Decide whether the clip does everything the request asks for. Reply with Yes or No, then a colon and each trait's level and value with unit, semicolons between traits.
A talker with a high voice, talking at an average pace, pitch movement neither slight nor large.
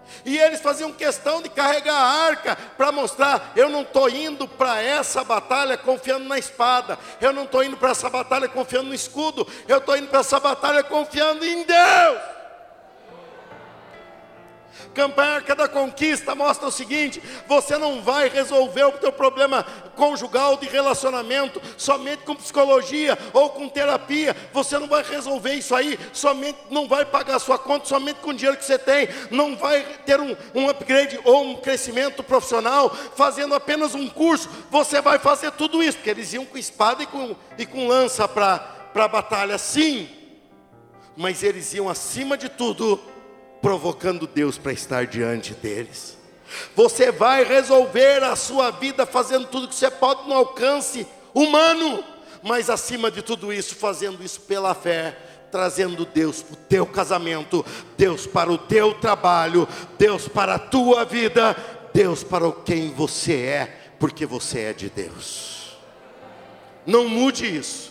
Yes: very high, 265 Hz; average, 160 wpm; average, 4.8 semitones